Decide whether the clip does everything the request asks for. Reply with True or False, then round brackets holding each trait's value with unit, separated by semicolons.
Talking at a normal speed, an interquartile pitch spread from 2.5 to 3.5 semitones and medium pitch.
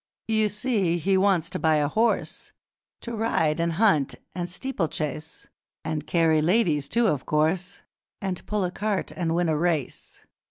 False (160 wpm; 4.7 semitones; 175 Hz)